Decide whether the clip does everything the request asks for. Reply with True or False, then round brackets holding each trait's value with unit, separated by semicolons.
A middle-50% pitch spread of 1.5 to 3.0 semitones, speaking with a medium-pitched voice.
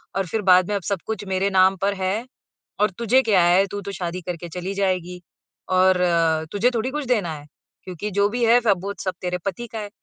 False (2.5 semitones; 195 Hz)